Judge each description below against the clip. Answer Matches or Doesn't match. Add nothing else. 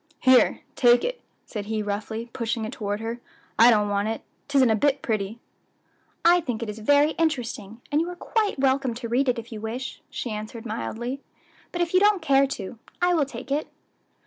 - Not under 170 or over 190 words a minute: Doesn't match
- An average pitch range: Matches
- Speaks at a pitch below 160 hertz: Doesn't match